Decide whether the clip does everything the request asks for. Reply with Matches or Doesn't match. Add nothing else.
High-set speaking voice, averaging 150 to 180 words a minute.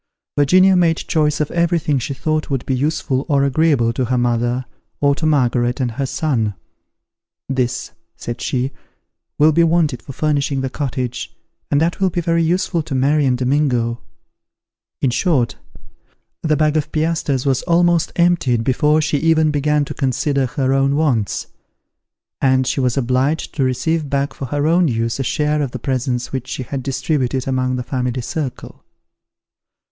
Doesn't match